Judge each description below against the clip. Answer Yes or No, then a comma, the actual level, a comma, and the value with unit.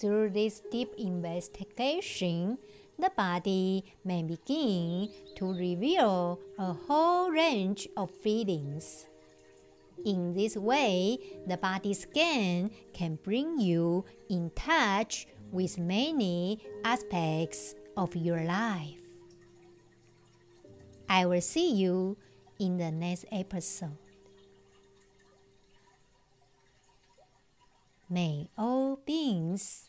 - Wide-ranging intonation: No, average, 3.9 semitones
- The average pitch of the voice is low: No, medium, 185 Hz